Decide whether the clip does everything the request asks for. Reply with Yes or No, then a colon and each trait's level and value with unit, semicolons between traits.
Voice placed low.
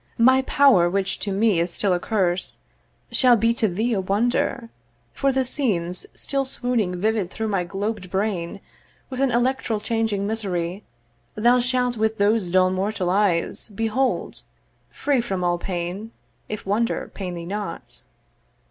No: high, 210 Hz